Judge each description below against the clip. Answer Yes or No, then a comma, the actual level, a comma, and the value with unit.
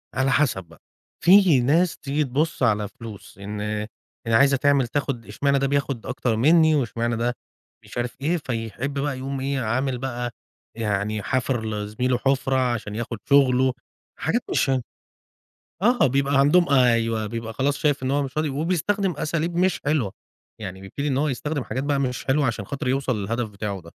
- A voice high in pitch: No, low, 130 Hz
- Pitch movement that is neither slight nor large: Yes, average, 3.7 semitones